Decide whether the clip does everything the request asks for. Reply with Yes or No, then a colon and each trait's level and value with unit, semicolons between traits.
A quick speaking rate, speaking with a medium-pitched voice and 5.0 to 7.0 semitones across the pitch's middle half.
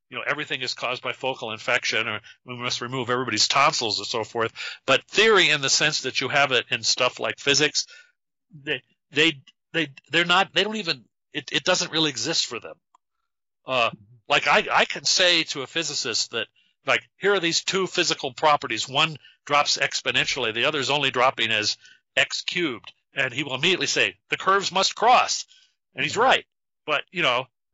No: average, 190 wpm; medium, 150 Hz; wide, 5.6 semitones